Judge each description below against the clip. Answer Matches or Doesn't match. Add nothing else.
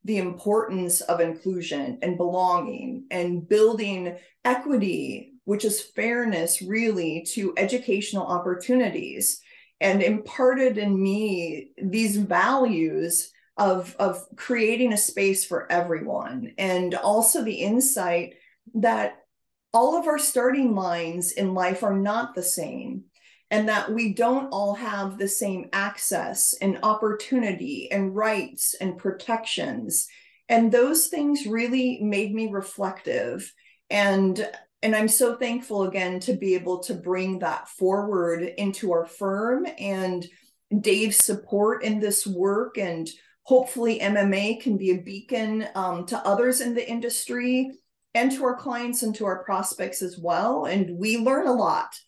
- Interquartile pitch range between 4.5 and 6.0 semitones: Doesn't match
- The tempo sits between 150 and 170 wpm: Doesn't match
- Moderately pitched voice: Doesn't match